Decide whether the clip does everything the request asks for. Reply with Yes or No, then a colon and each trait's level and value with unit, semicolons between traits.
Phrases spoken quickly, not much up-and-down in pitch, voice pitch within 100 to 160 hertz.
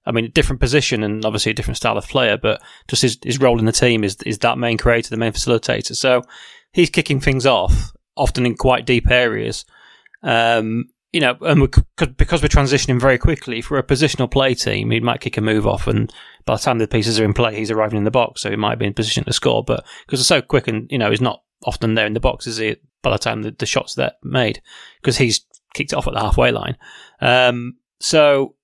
No: fast, 245 wpm; average, 3.0 semitones; low, 120 Hz